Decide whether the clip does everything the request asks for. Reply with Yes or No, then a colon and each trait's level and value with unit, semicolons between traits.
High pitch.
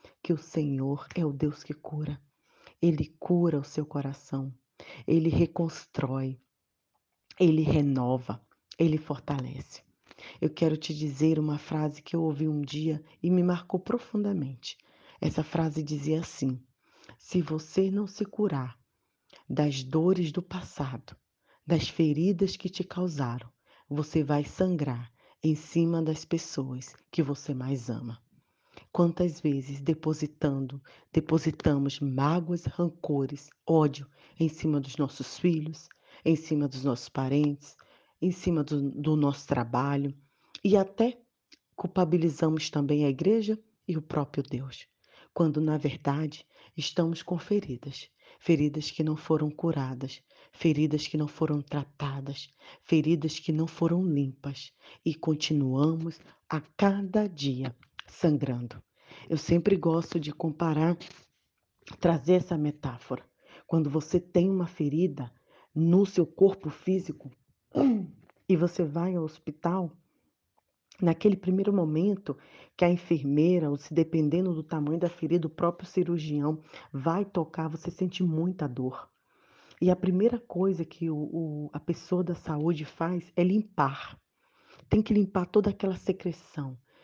No: medium, 155 Hz